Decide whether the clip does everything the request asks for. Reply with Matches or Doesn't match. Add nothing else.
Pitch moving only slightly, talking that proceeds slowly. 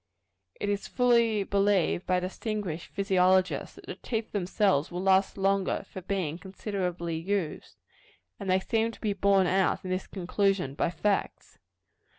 Doesn't match